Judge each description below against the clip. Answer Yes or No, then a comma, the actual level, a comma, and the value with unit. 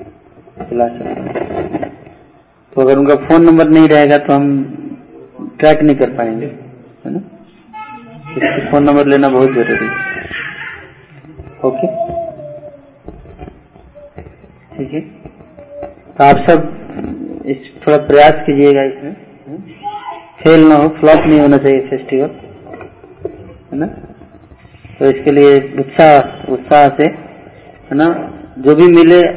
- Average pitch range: Yes, average, 3.7 semitones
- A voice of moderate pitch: Yes, medium, 150 Hz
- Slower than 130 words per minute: Yes, average, 115 wpm